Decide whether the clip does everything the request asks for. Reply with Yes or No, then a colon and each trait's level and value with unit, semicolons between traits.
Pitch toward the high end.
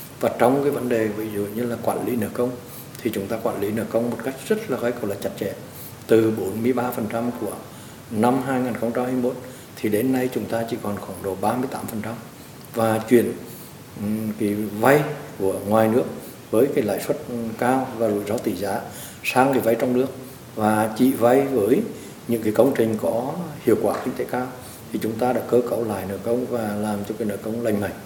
No: low, 115 Hz